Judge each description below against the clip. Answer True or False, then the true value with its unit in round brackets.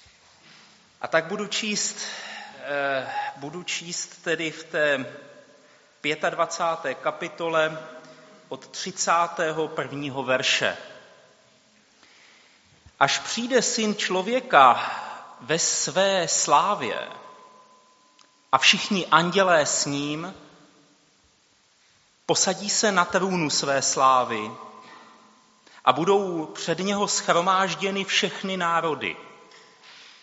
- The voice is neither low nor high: True (170 Hz)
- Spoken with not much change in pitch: False (4.4 semitones)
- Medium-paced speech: False (75 wpm)